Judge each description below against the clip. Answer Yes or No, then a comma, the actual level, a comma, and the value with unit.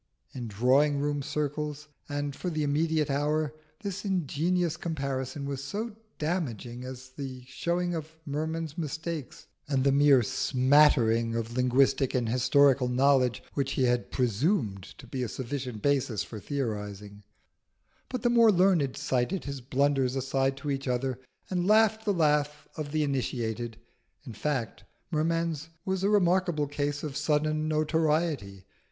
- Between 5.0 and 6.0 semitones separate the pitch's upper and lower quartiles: No, average, 3.6 semitones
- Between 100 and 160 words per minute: Yes, average, 145 wpm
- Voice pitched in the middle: Yes, medium, 145 Hz